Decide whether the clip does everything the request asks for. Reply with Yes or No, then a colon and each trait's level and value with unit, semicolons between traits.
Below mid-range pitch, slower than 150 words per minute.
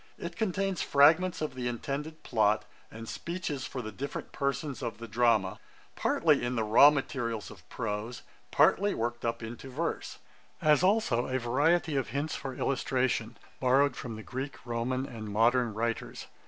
No: low, 125 Hz; average, 160 wpm